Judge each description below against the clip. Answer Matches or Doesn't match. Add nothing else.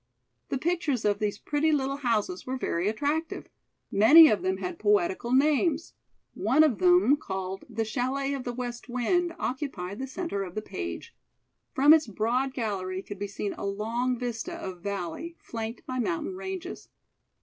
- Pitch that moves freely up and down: Matches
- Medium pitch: Doesn't match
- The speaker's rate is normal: Matches